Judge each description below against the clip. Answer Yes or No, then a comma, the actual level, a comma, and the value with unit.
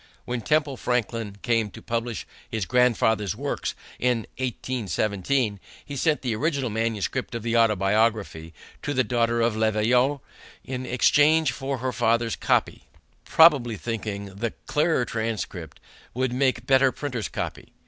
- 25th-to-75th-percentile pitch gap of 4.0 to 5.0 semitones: No, average, 3.0 semitones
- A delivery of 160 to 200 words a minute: No, average, 140 wpm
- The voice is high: No, low, 120 Hz